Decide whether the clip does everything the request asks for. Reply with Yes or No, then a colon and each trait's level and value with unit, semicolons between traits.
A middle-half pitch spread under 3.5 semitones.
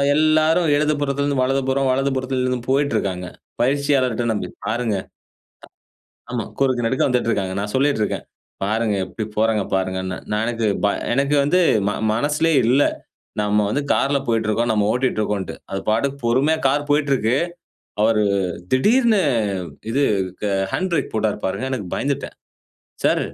No: average, 4.6 semitones